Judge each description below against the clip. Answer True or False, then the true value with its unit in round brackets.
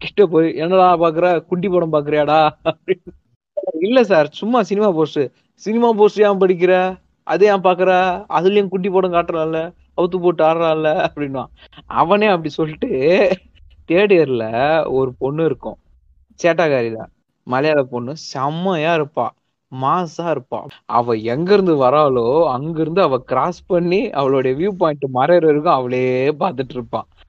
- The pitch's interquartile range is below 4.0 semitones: False (5.5 semitones)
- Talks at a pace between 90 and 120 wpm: False (130 wpm)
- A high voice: False (160 Hz)